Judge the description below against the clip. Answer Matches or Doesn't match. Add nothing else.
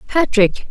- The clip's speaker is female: Matches